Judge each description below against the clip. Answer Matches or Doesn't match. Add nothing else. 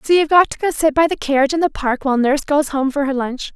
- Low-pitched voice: Doesn't match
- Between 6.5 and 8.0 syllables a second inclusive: Matches